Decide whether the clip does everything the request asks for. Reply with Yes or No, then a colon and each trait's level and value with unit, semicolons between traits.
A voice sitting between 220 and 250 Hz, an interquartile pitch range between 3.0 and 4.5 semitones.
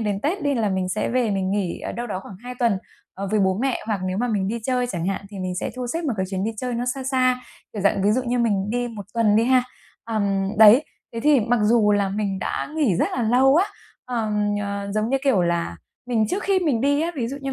Yes: high, 225 Hz; average, 4.1 semitones